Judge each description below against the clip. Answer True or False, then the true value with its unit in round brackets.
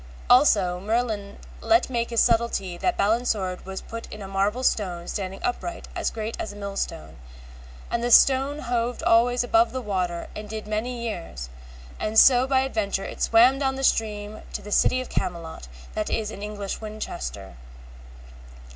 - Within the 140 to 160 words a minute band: False (175 wpm)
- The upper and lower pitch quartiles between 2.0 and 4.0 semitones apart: True (3.7 semitones)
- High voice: True (215 Hz)